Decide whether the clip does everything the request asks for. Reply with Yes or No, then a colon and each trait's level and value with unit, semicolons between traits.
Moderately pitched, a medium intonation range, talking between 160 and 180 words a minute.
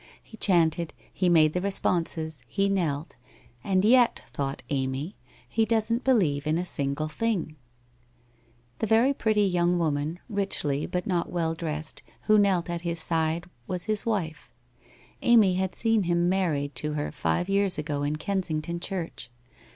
Yes: medium, 170 Hz; average, 4.5 semitones; average, 165 wpm